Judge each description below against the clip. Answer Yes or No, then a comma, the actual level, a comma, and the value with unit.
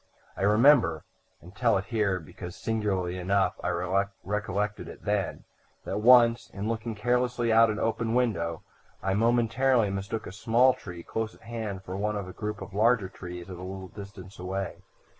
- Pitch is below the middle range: Yes, low, 105 Hz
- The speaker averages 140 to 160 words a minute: No, average, 180 wpm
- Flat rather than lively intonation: No, average, 3.3 semitones